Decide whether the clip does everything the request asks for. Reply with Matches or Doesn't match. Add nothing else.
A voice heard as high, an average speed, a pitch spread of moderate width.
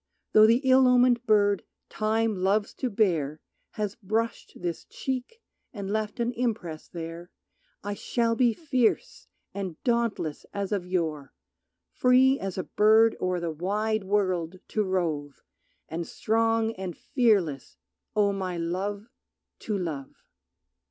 Doesn't match